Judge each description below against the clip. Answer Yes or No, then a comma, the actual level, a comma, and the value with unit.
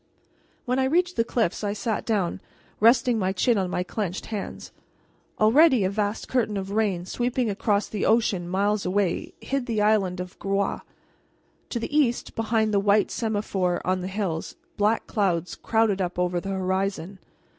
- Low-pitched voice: No, high, 205 Hz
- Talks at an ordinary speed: Yes, average, 165 wpm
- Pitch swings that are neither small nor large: Yes, average, 3.1 semitones